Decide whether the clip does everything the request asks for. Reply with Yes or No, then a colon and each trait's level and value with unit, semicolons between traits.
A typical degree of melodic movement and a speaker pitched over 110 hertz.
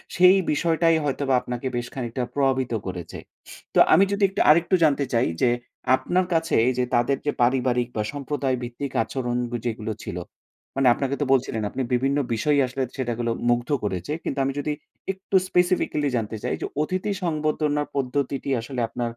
Yes: average, 3.7 semitones; low, 135 Hz